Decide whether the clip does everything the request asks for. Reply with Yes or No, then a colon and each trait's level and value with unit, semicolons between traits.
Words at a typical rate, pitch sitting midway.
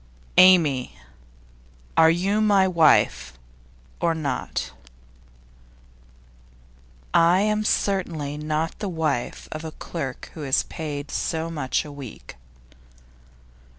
No: slow, 100 wpm; medium, 160 Hz